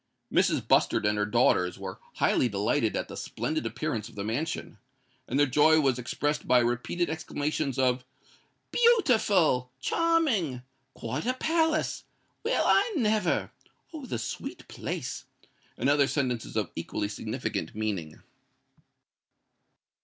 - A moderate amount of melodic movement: No, wide, 7.5 semitones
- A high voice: No, low, 135 Hz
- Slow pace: Yes, slow, 115 wpm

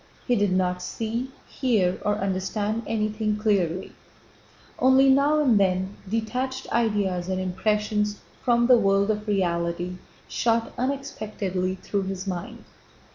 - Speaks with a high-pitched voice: Yes, high, 210 Hz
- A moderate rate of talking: No, slow, 125 wpm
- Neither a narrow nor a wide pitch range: Yes, average, 3.5 semitones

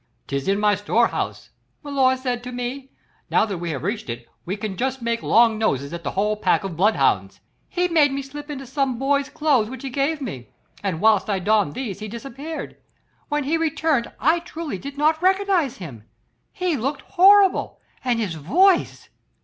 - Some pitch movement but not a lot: No, wide, 6.1 semitones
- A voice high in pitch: Yes, very high, 255 Hz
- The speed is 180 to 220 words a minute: Yes, average, 190 wpm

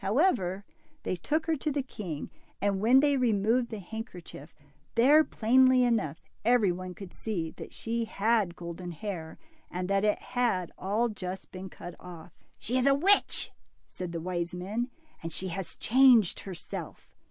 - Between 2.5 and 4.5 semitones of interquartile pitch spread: No, wide, 5.4 semitones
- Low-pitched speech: No, high, 205 Hz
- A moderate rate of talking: Yes, average, 165 wpm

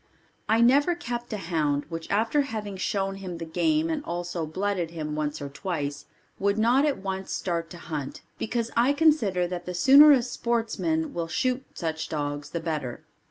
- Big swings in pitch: Yes, wide, 6.7 semitones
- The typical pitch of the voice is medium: No, high, 195 Hz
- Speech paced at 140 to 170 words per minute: No, average, 180 wpm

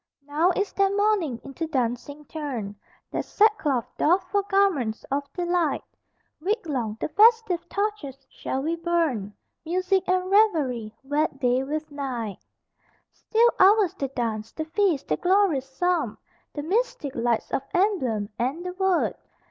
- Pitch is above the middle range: Yes, very high, 315 Hz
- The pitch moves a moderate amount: No, wide, 6.3 semitones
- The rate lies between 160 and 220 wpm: No, average, 140 wpm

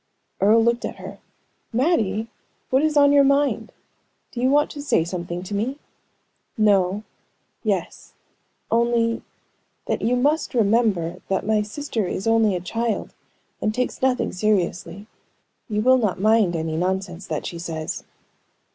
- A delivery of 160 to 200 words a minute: No, average, 145 wpm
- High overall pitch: Yes, high, 220 Hz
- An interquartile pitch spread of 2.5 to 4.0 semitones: No, average, 4.8 semitones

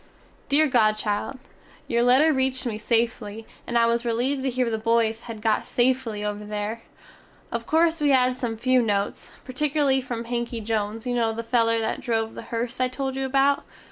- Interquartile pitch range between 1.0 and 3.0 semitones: Yes, average, 2.7 semitones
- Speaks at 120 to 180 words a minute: No, average, 190 wpm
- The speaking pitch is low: No, high, 235 Hz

